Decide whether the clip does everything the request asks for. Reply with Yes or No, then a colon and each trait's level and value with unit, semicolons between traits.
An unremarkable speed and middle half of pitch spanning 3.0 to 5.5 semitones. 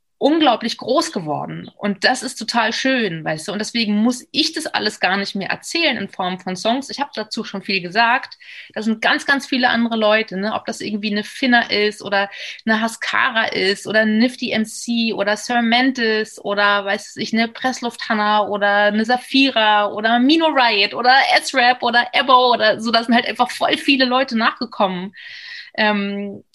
Yes: average, 180 wpm; average, 3.3 semitones